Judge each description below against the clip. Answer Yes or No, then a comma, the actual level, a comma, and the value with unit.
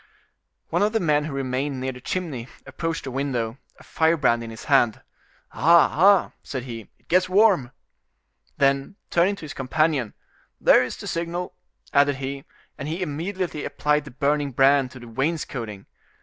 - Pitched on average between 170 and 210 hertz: No, medium, 145 Hz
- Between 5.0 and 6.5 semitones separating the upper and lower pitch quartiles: No, average, 4.3 semitones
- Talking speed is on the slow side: No, average, 165 wpm